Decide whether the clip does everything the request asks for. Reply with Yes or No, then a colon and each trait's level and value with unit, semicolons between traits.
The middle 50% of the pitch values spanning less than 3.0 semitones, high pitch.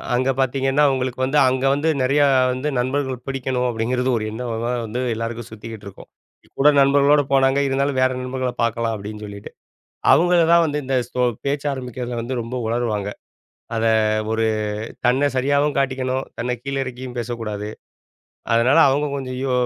No: narrow, 2.6 semitones; low, 130 Hz